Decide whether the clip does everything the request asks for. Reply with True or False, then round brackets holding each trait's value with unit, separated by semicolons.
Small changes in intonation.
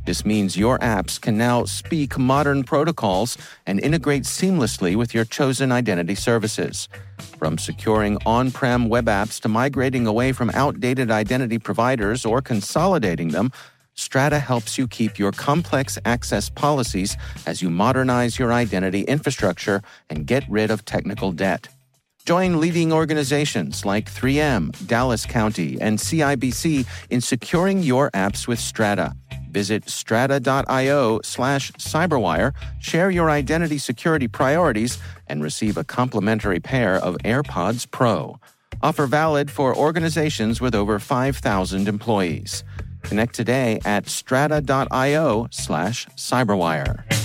False (5.0 semitones)